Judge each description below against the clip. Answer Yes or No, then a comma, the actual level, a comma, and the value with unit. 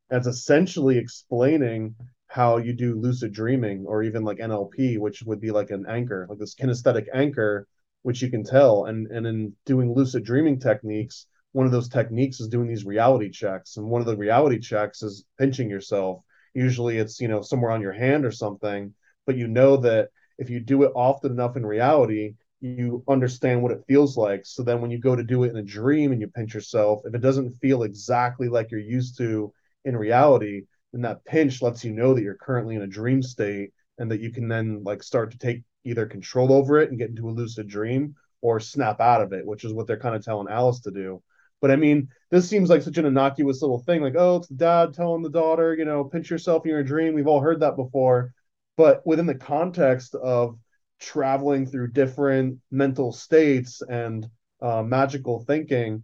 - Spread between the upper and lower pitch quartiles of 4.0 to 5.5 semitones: No, average, 3.6 semitones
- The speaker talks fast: Yes, fast, 210 wpm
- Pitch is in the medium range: No, low, 125 Hz